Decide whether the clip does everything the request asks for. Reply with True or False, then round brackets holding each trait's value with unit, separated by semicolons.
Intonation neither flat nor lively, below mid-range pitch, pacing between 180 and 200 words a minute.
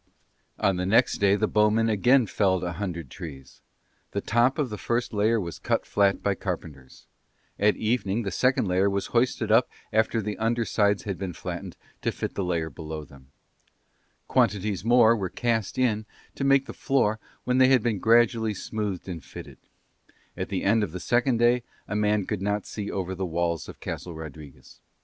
True (3.9 semitones; 105 Hz; 185 wpm)